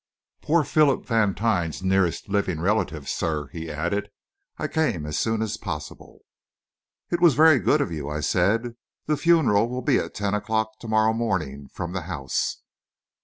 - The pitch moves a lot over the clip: Yes, wide, 6.0 semitones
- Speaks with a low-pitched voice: Yes, low, 105 Hz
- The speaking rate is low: No, average, 165 wpm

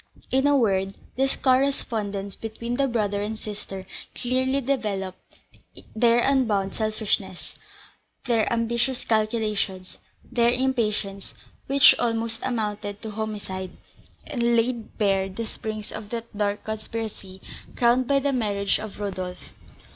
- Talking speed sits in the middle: No, slow, 120 wpm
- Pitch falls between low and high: No, high, 220 Hz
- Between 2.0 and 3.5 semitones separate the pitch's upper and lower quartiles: Yes, average, 2.9 semitones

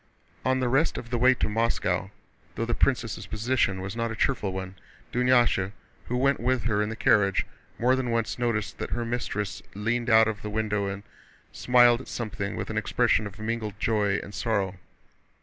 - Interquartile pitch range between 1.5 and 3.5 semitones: Yes, average, 2.9 semitones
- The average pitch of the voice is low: Yes, low, 115 Hz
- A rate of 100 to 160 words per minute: No, average, 190 wpm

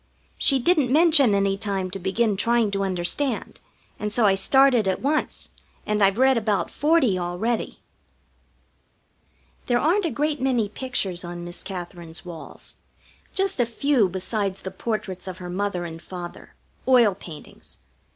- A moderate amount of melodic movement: No, wide, 5.7 semitones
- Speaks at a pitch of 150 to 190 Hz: No, high, 205 Hz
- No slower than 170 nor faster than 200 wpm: No, average, 150 wpm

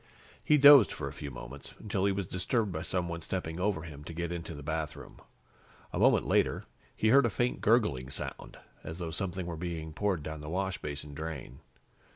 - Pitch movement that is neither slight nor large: Yes, average, 3.9 semitones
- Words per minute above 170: Yes, average, 190 wpm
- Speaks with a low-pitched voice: Yes, very low, 85 Hz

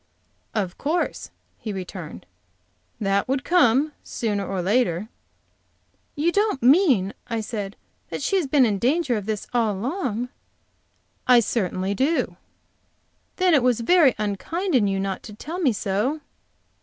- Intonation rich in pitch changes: Yes, wide, 6.6 semitones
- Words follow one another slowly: No, average, 145 wpm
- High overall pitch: Yes, high, 235 Hz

